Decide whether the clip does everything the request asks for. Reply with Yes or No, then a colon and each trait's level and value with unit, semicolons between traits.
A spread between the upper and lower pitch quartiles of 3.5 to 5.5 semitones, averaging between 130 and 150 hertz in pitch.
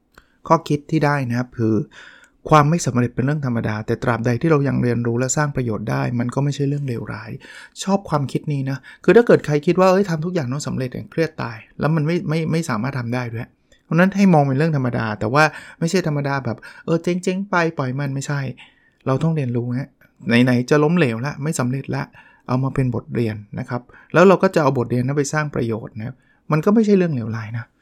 Yes: average, 4.7 semitones; medium, 140 Hz